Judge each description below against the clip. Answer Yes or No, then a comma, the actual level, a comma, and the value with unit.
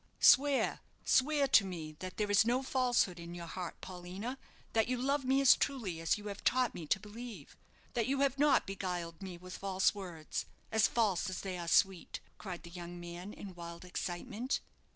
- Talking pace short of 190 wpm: No, average, 195 wpm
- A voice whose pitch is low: No, high, 195 Hz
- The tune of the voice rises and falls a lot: Yes, wide, 5.9 semitones